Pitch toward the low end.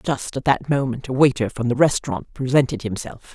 Yes: low, 130 Hz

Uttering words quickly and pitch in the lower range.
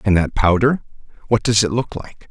Yes: fast, 210 wpm; low, 110 Hz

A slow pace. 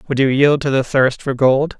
No: fast, 265 wpm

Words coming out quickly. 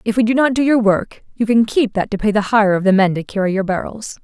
Yes: fast, 310 wpm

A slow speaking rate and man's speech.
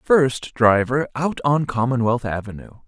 Yes: slow, 125 wpm; male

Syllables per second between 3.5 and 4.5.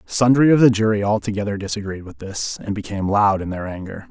No: 6.1 syllables/s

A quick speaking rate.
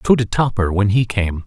Yes: fast, 245 wpm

